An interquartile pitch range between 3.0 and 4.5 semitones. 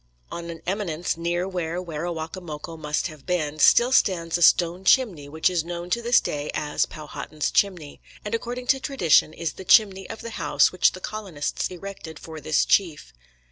Yes: average, 3.6 semitones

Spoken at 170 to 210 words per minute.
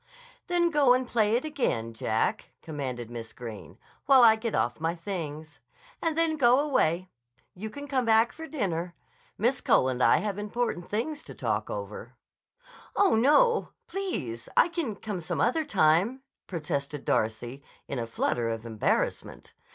No: average, 160 wpm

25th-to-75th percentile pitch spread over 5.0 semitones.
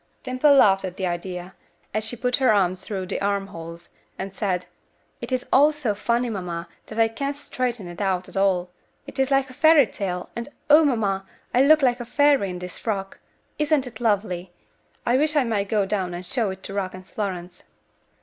Yes: wide, 5.4 semitones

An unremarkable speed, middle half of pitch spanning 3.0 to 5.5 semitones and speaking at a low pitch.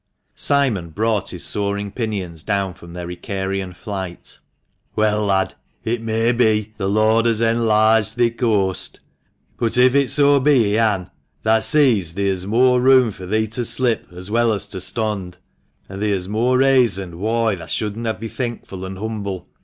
Yes: average, 160 wpm; average, 3.3 semitones; low, 110 Hz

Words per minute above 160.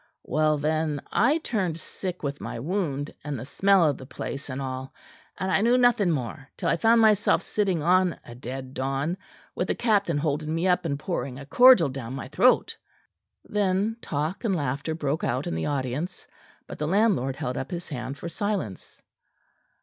Yes: average, 185 wpm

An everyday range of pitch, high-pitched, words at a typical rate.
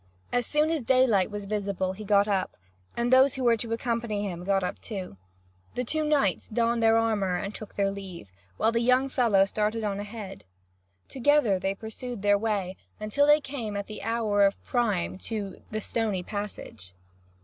Yes: average, 3.2 semitones; high, 215 Hz; average, 180 wpm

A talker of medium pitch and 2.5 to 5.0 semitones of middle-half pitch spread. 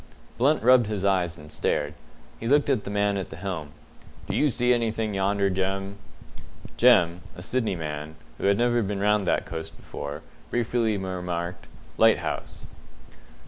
No: low, 100 Hz; average, 4.5 semitones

